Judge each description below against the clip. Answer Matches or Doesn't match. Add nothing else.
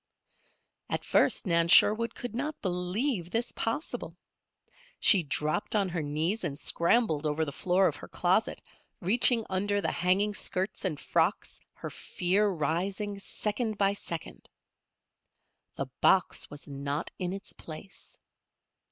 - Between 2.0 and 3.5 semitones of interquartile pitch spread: Doesn't match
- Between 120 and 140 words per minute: Matches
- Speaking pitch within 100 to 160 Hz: Doesn't match